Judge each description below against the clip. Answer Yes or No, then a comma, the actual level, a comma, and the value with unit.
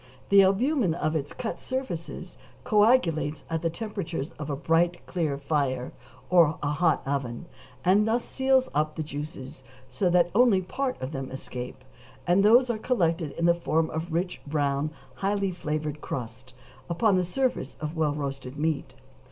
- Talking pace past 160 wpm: Yes, average, 170 wpm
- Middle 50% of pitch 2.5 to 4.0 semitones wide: No, average, 5.1 semitones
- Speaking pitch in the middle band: Yes, medium, 165 Hz